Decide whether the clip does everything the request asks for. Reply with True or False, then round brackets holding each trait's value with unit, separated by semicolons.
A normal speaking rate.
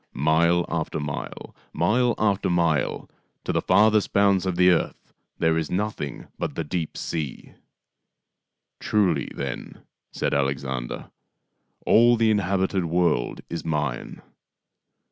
False (130 wpm)